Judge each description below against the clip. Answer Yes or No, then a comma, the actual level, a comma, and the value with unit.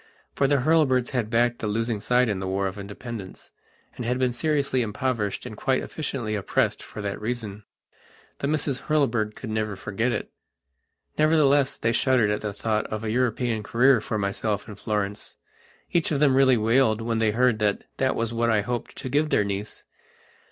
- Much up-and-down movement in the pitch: No, average, 3.7 semitones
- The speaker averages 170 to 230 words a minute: Yes, average, 185 wpm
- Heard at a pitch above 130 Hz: No, low, 115 Hz